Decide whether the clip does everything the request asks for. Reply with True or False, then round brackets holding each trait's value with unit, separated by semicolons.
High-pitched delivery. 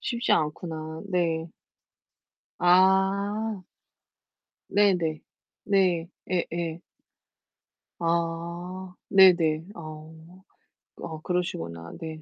False (170 Hz)